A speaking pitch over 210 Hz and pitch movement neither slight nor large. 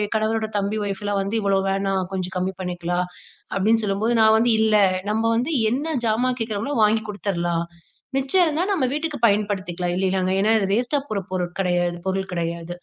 No: high, 200 Hz; average, 3.5 semitones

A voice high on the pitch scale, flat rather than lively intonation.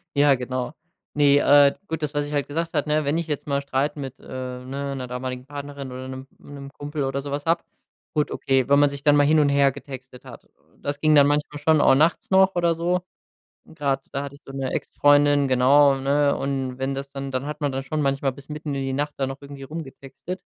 No: medium, 140 Hz; narrow, 1.5 semitones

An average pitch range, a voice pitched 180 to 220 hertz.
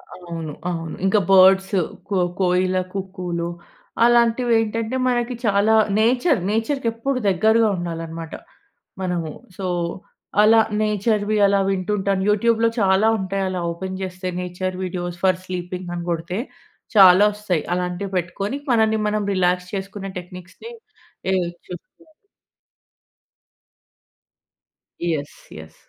Yes: average, 3.5 semitones; high, 190 Hz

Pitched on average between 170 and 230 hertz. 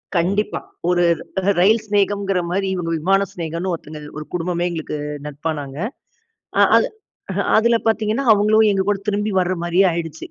Yes: medium, 185 Hz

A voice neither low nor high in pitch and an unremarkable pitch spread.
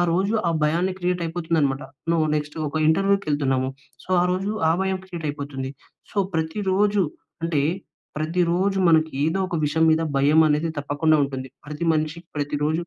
Yes: medium, 160 Hz; average, 3.4 semitones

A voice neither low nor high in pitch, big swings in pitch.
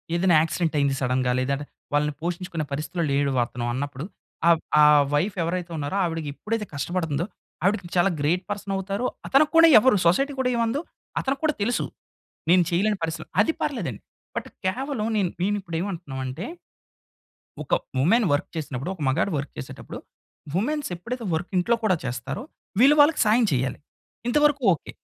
Yes: medium, 175 Hz; wide, 6.6 semitones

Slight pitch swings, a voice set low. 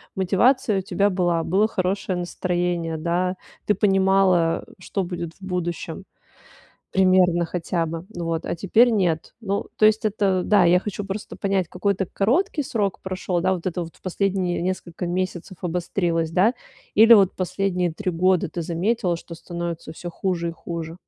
No: narrow, 2.3 semitones; medium, 185 Hz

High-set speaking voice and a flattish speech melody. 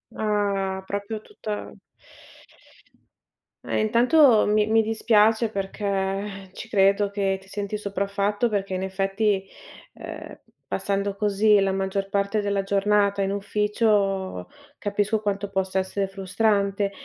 Yes: high, 200 Hz; narrow, 1.3 semitones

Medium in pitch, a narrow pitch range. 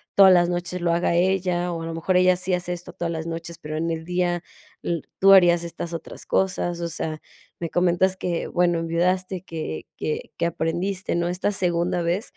Yes: medium, 175 Hz; narrow, 1.4 semitones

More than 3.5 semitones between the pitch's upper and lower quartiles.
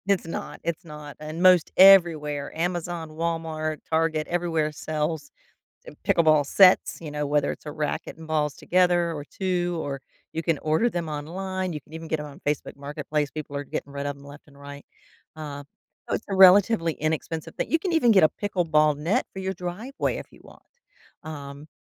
No: average, 3.0 semitones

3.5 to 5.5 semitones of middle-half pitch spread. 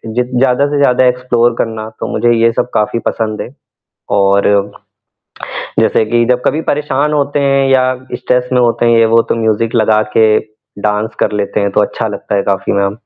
No: average, 2.9 semitones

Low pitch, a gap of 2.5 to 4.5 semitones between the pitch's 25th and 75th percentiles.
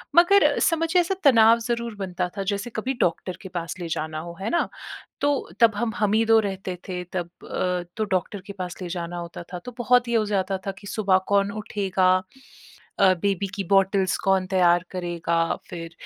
No: high, 195 Hz; average, 3.7 semitones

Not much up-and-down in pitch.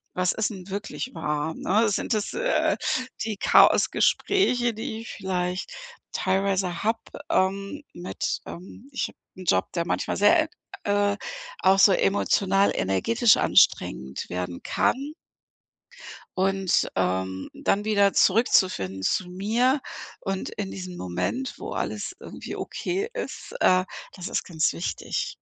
No: average, 3.9 semitones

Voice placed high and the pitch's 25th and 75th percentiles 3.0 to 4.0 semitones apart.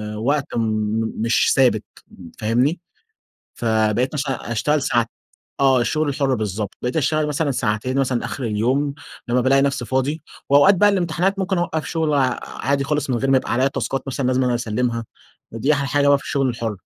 No: low, 135 Hz; average, 3.4 semitones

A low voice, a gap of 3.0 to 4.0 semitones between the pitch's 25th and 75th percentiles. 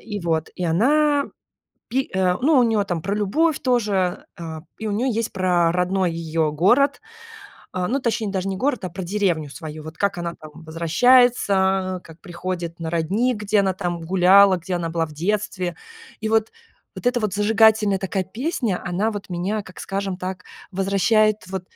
No: high, 190 Hz; average, 3.7 semitones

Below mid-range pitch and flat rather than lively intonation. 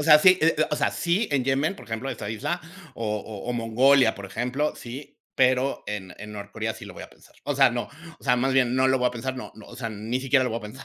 No: low, 125 Hz; average, 3.5 semitones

